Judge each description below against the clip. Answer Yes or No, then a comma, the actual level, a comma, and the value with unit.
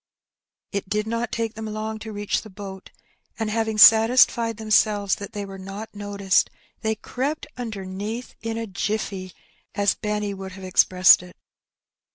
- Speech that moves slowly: No, average, 155 wpm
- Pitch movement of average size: No, narrow, 2.2 semitones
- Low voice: No, high, 210 Hz